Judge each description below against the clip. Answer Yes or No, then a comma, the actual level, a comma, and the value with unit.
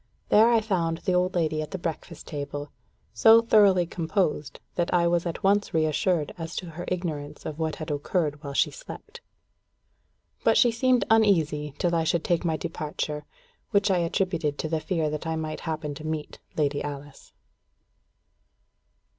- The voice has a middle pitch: Yes, medium, 165 Hz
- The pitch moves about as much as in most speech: Yes, average, 3.4 semitones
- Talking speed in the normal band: Yes, average, 170 wpm